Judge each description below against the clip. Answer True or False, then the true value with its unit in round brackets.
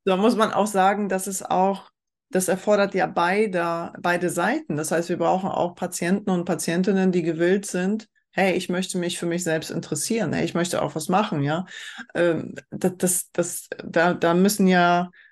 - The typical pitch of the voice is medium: True (180 Hz)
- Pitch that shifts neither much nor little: False (2.2 semitones)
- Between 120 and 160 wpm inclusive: False (185 wpm)